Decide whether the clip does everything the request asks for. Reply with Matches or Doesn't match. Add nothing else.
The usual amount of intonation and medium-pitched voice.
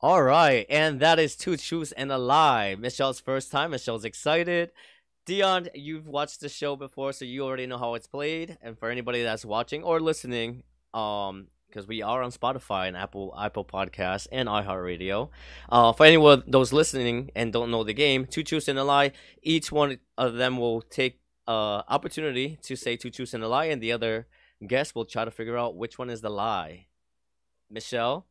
Doesn't match